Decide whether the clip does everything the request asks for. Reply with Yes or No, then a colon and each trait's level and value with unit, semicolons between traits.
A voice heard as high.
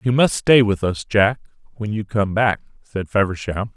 No: low, 105 Hz